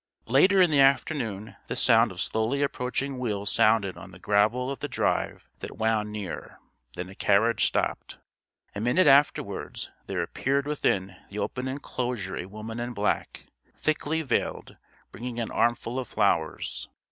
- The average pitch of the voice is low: Yes, low, 120 Hz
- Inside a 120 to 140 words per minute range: No, average, 155 wpm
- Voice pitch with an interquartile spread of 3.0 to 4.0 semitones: No, average, 4.6 semitones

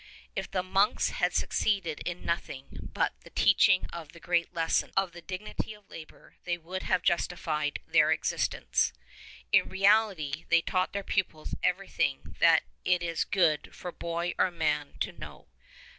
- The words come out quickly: No, average, 160 wpm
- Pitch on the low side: No, medium, 175 Hz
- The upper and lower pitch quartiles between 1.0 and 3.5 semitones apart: Yes, narrow, 2.5 semitones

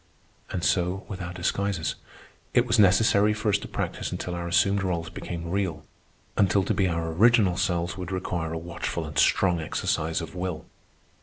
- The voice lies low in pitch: Yes, very low, 90 Hz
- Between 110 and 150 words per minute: No, average, 175 wpm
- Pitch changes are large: No, average, 2.7 semitones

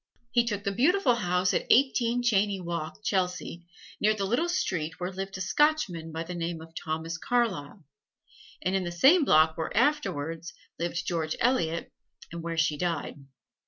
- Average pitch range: No, wide, 6.0 semitones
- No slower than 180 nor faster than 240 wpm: No, average, 165 wpm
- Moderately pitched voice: Yes, medium, 180 Hz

